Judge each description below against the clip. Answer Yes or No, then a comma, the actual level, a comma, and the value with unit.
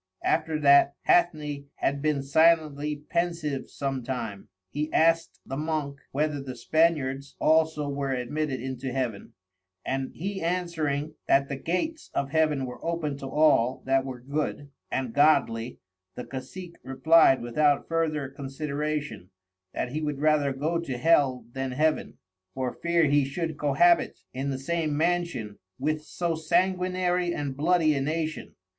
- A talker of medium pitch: Yes, medium, 150 Hz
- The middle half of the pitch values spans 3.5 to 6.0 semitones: No, average, 3.1 semitones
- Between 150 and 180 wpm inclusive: No, average, 140 wpm